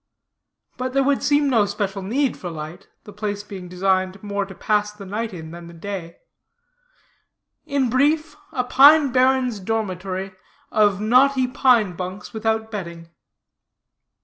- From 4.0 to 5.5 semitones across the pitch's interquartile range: Yes, average, 5.1 semitones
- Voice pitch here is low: No, high, 210 Hz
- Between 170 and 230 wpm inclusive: No, average, 145 wpm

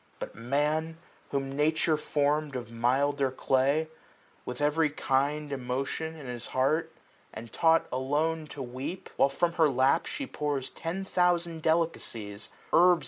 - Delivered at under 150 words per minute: Yes, average, 140 wpm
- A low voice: No, medium, 145 Hz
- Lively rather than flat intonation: No, average, 3.5 semitones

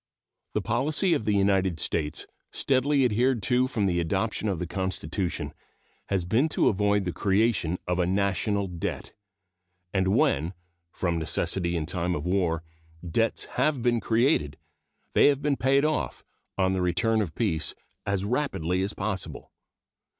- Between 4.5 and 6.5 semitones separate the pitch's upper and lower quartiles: Yes, average, 4.8 semitones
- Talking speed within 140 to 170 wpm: Yes, average, 150 wpm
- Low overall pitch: Yes, low, 100 Hz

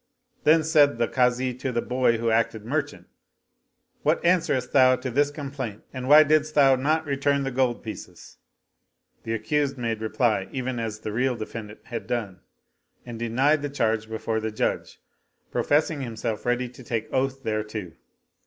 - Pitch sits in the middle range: No, low, 125 Hz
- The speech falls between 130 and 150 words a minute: No, average, 170 wpm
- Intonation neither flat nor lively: Yes, average, 3.8 semitones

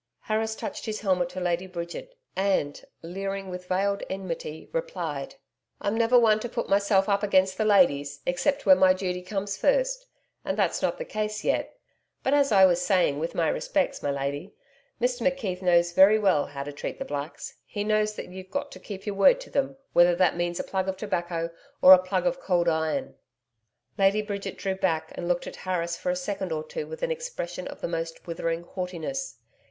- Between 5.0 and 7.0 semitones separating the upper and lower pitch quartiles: No, average, 3.7 semitones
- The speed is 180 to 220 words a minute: Yes, average, 200 wpm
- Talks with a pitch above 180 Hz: Yes, high, 190 Hz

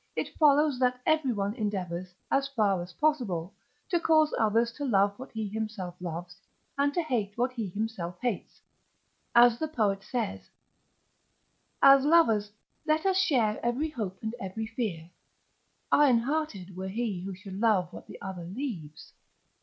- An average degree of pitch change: No, wide, 6.0 semitones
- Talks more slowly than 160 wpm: Yes, average, 150 wpm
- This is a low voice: No, high, 225 Hz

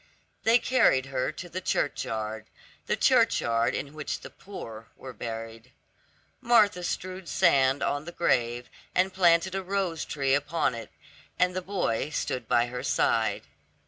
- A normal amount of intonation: No, wide, 7.6 semitones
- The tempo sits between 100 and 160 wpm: Yes, average, 145 wpm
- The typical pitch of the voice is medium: Yes, medium, 145 Hz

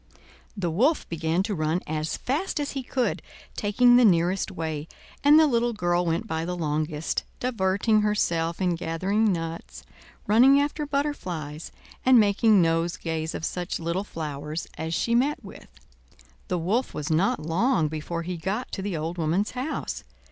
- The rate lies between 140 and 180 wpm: Yes, average, 160 wpm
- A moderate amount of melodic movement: No, wide, 6.1 semitones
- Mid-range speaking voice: Yes, medium, 180 Hz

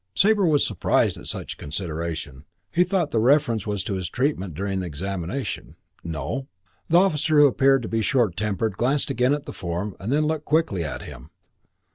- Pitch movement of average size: No, wide, 8.2 semitones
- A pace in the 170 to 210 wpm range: Yes, average, 180 wpm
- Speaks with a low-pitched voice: Yes, low, 115 Hz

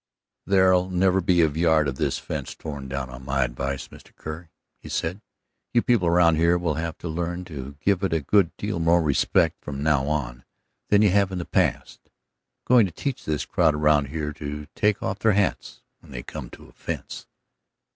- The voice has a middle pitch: No, very low, 80 Hz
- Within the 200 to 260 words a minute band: Yes, fast, 205 wpm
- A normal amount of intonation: Yes, average, 4.2 semitones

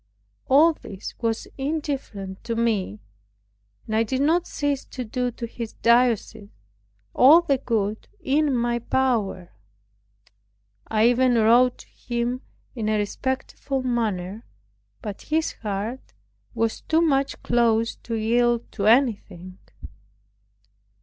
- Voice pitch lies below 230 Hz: No, high, 235 Hz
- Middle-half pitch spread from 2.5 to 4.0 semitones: Yes, average, 3.4 semitones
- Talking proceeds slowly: Yes, slow, 120 wpm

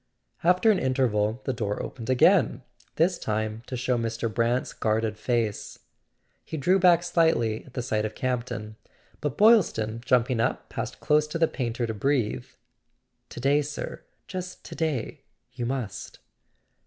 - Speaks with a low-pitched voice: Yes, low, 125 Hz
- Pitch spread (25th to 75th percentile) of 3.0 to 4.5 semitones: No, average, 5.0 semitones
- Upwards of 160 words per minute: No, average, 150 wpm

